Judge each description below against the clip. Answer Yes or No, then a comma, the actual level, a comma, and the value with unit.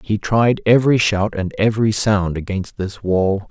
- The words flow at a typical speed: Yes, average, 170 wpm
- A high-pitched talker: No, low, 105 Hz